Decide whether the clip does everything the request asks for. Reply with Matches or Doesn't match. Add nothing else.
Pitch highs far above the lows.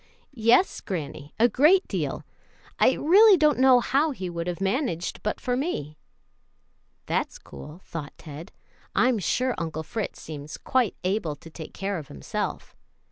Matches